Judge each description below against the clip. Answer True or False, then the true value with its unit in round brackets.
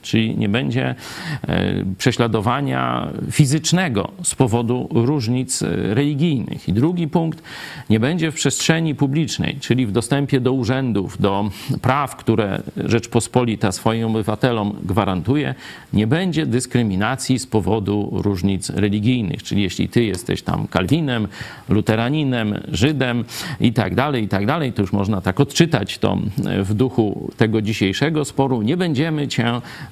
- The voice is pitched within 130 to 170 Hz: False (120 Hz)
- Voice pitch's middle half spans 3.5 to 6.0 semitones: True (4.9 semitones)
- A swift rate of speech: False (130 wpm)